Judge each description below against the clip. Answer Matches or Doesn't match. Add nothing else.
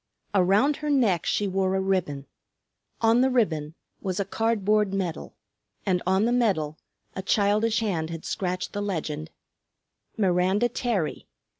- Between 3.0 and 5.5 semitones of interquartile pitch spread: Matches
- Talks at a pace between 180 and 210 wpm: Doesn't match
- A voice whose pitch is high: Matches